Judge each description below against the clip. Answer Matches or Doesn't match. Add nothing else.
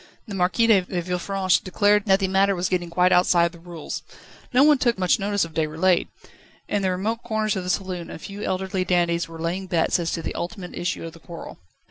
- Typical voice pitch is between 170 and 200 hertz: Matches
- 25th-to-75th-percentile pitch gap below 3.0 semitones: Matches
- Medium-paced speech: Doesn't match